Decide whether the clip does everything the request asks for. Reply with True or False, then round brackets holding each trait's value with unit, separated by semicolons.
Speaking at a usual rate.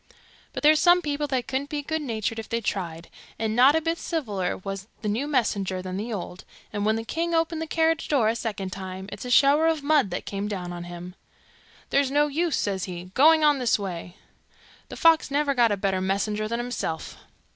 False (210 wpm)